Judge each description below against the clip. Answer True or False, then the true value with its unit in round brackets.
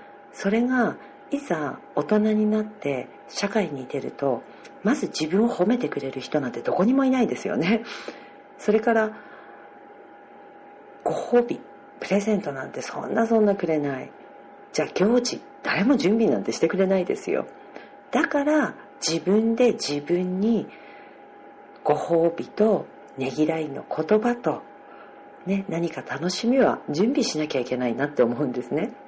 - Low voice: False (200 Hz)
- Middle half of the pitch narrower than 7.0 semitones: True (6.5 semitones)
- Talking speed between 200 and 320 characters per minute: True (280 characters per minute)